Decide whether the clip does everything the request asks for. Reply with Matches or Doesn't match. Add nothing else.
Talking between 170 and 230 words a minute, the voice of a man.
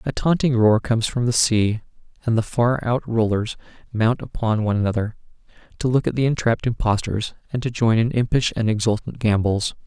Matches